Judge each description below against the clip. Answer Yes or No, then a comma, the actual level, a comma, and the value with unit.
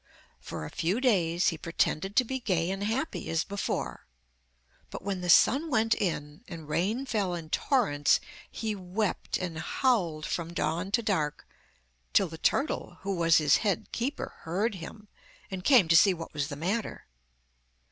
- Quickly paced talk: No, average, 165 wpm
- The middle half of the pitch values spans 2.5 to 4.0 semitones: No, average, 5.0 semitones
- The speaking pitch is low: No, medium, 185 Hz